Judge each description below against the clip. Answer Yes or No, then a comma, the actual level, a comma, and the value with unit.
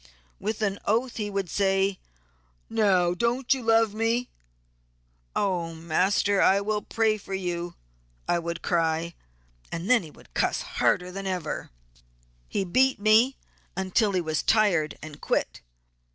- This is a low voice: No, high, 195 Hz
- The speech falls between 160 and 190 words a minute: No, average, 140 wpm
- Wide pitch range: No, average, 3.8 semitones